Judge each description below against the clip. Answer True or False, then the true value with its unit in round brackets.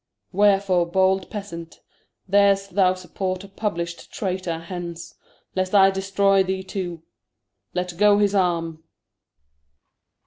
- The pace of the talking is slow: True (110 wpm)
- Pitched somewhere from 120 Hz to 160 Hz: False (190 Hz)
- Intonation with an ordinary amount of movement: False (2.1 semitones)